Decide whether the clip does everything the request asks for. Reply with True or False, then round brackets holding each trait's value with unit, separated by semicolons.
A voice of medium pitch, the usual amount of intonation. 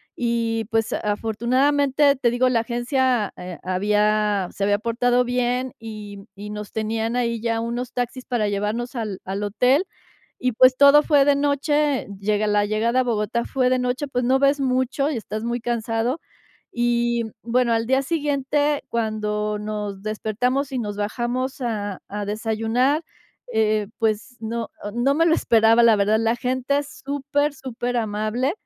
False (235 Hz; 3.2 semitones)